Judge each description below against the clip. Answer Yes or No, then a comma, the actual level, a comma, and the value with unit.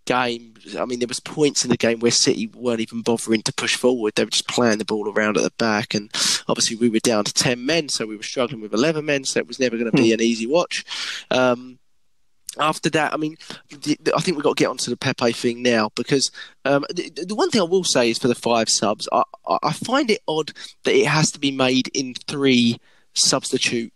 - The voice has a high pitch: No, low, 125 Hz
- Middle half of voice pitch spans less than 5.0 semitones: Yes, average, 3.6 semitones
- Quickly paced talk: Yes, fast, 250 wpm